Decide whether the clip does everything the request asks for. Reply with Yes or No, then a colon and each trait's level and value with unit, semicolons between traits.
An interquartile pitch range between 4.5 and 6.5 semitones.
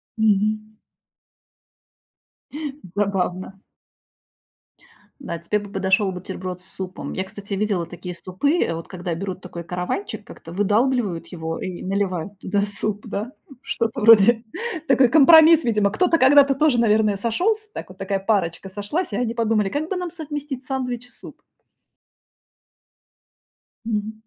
Yes: average, 4.9 semitones